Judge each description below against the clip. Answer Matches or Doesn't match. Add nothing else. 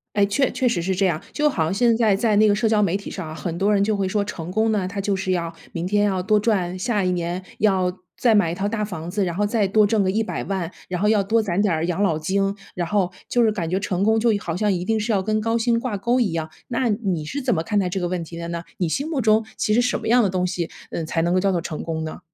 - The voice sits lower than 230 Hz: Matches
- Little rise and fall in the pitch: Doesn't match